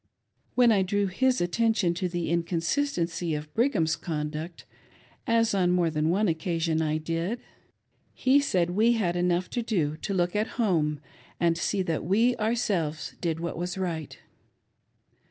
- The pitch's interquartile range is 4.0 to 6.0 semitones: Yes, average, 4.4 semitones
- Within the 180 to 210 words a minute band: No, average, 155 wpm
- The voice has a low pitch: No, medium, 175 Hz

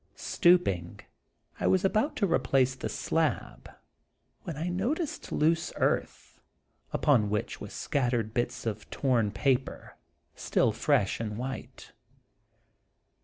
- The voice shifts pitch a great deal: Yes, wide, 7.4 semitones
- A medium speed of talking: No, slow, 115 wpm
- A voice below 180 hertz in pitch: Yes, low, 135 Hz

